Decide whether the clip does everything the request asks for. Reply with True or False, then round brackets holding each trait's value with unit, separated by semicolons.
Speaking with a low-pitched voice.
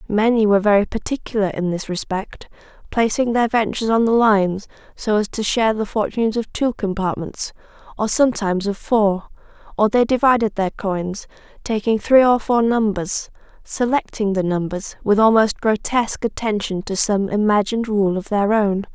False (210 Hz)